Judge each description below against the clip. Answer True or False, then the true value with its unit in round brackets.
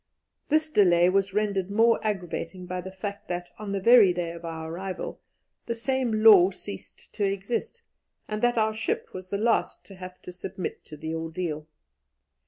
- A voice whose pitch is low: False (195 Hz)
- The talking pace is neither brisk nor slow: True (180 wpm)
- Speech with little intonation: False (3.4 semitones)